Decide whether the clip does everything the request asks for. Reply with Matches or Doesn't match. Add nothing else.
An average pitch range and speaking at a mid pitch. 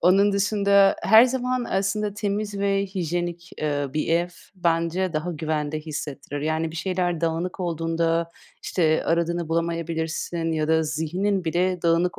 Matches